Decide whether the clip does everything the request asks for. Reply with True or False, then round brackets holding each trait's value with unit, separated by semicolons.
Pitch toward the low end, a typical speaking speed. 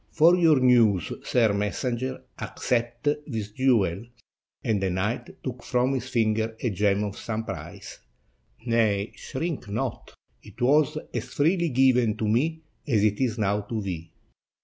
True (115 Hz; 150 wpm)